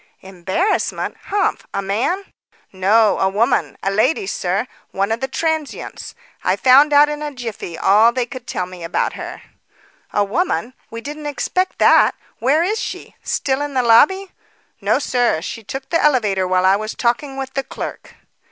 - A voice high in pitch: Yes, very high, 250 Hz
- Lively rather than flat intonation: Yes, wide, 6.5 semitones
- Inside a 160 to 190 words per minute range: Yes, average, 170 wpm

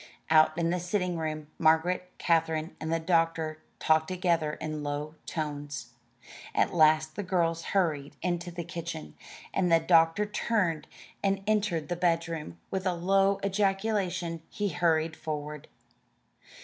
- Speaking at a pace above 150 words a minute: No, slow, 135 wpm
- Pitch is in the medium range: Yes, medium, 165 Hz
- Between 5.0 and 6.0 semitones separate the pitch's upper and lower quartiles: No, narrow, 2.6 semitones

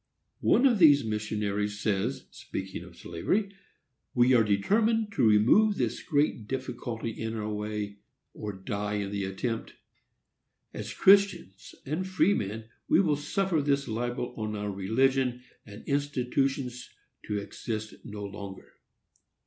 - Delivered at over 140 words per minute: No, slow, 135 wpm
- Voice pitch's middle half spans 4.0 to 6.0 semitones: Yes, wide, 5.4 semitones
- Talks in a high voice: No, low, 115 Hz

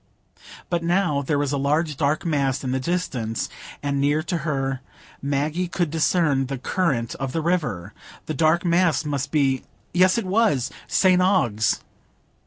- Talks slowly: No, average, 150 wpm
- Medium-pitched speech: Yes, medium, 150 Hz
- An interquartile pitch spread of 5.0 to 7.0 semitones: No, average, 4.2 semitones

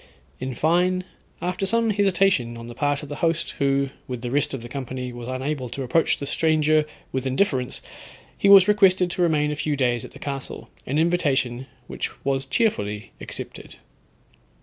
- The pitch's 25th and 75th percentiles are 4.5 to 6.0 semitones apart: Yes, average, 5.3 semitones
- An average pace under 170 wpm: No, average, 175 wpm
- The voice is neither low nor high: Yes, medium, 145 Hz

